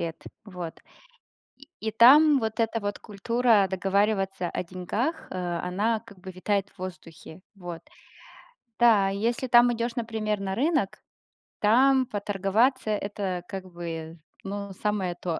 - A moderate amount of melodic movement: Yes, average, 3.7 semitones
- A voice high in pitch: Yes, high, 205 Hz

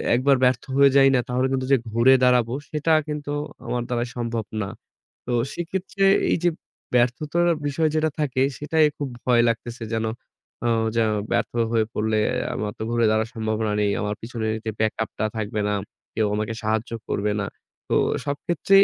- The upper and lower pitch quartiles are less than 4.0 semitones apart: No, average, 4.4 semitones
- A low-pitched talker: Yes, low, 120 Hz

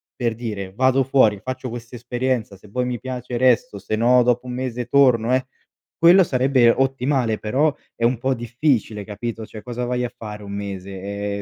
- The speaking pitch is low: Yes, low, 120 Hz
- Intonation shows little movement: No, average, 3.1 semitones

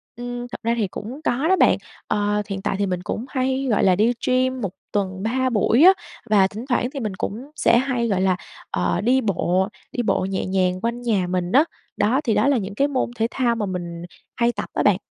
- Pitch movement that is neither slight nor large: Yes, average, 4.7 semitones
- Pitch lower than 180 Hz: No, high, 225 Hz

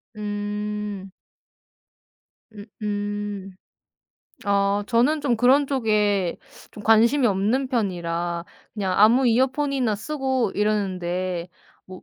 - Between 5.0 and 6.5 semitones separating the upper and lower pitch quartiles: No, average, 3.7 semitones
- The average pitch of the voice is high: Yes, high, 210 Hz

